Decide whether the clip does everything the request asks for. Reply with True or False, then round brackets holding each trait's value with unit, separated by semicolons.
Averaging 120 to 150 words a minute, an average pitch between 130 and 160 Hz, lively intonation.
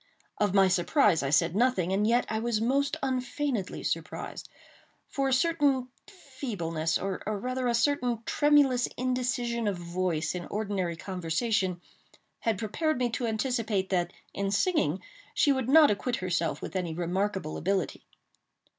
False (145 wpm; 215 Hz; 5.7 semitones)